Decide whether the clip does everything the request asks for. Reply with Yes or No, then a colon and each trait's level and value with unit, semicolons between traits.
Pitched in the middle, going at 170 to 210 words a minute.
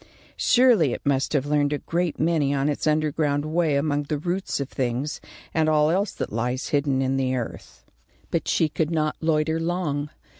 Yes: medium, 150 Hz; average, 185 wpm